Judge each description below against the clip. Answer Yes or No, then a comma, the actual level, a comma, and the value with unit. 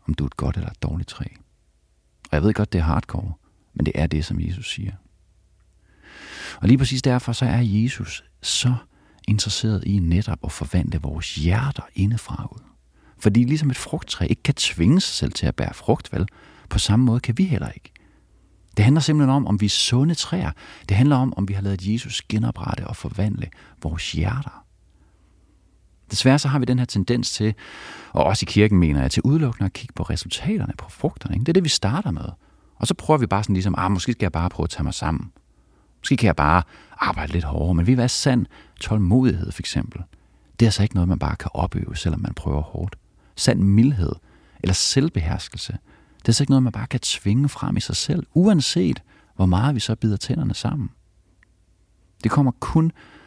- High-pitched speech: No, low, 105 Hz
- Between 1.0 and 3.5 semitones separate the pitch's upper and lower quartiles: No, wide, 5.5 semitones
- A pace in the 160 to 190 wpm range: No, fast, 205 wpm